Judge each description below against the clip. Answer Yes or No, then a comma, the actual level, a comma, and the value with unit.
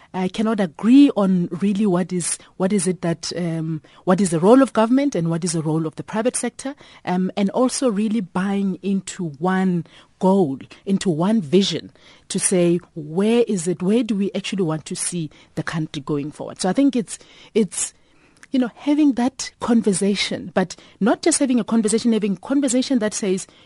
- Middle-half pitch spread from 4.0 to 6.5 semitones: Yes, average, 4.5 semitones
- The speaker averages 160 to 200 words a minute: Yes, average, 190 wpm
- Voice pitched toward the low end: No, high, 195 Hz